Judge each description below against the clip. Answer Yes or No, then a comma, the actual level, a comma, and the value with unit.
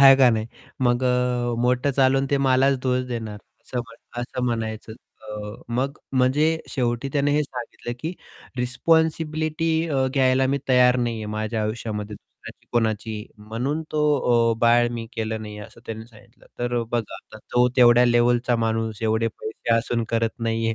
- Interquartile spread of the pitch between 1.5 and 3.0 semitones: Yes, narrow, 2.5 semitones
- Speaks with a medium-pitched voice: No, low, 120 Hz